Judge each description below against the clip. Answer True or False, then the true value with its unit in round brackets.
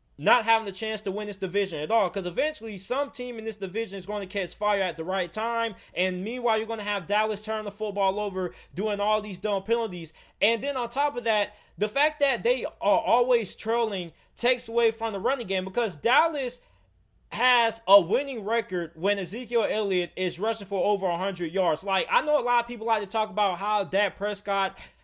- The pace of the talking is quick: True (215 wpm)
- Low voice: False (210 Hz)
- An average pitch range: True (3.0 semitones)